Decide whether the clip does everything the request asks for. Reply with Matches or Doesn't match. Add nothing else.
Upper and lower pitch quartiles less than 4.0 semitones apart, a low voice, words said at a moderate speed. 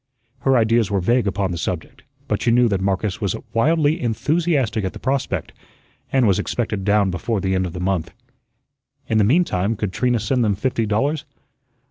Doesn't match